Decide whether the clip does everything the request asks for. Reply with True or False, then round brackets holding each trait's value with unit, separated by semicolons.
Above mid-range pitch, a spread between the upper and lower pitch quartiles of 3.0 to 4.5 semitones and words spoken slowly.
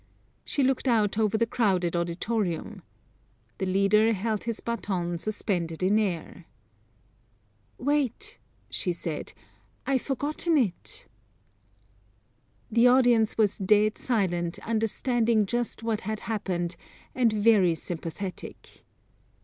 True (215 Hz; 4.0 semitones; 105 wpm)